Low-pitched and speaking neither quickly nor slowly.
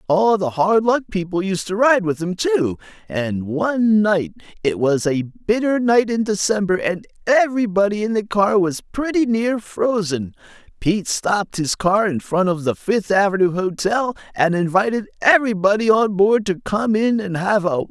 No: high, 200 Hz; average, 175 wpm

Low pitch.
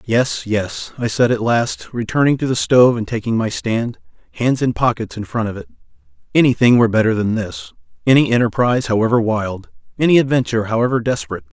Yes: low, 120 Hz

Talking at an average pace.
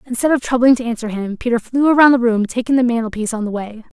No: fast, 255 wpm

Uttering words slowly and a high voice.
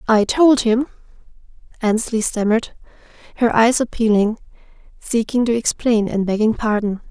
Yes: slow, 120 wpm; high, 225 Hz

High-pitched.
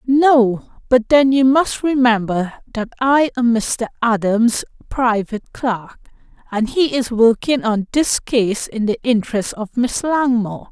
Yes: high, 235 Hz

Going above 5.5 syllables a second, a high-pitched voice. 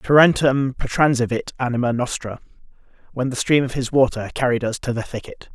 No: 5.7 syllables/s; low, 125 Hz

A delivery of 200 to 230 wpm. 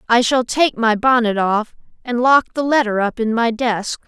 Yes: fast, 205 wpm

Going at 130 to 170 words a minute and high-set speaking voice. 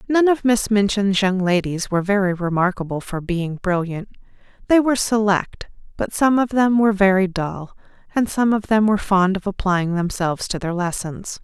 No: average, 180 wpm; high, 195 Hz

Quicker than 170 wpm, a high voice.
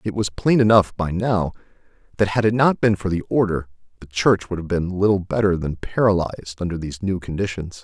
No: fast, 205 wpm; very low, 95 Hz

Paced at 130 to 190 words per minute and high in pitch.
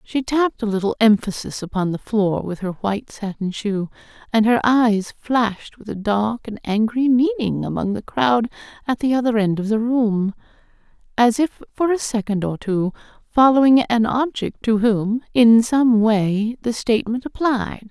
Yes: average, 170 wpm; high, 225 Hz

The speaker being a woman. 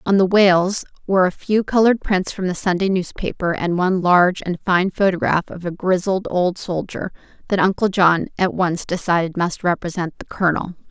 Yes: female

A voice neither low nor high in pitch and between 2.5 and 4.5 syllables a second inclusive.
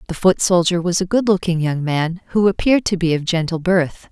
No: medium, 175 Hz; 5.5 syllables/s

